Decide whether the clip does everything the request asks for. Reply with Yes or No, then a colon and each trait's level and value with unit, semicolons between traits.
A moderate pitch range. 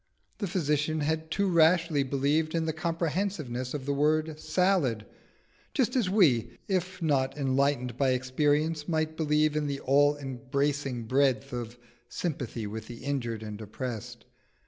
Yes: average, 3.8 semitones